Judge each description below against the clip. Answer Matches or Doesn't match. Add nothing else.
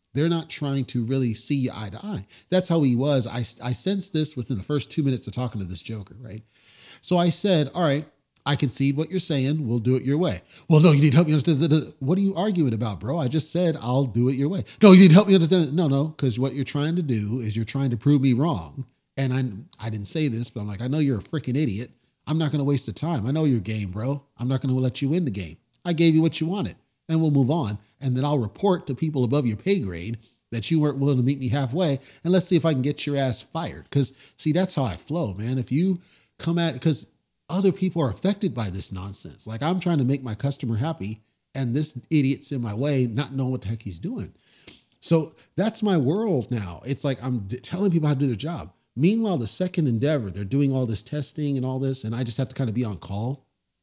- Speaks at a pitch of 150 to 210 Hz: Doesn't match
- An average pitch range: Matches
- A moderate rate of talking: Doesn't match